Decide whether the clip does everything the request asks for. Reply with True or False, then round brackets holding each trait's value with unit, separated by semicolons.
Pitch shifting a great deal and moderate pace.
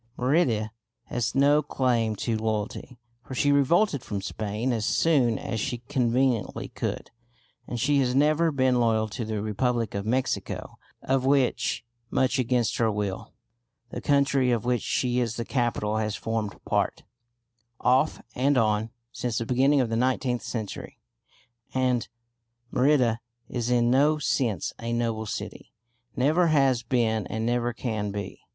False (3.0 semitones; 150 wpm)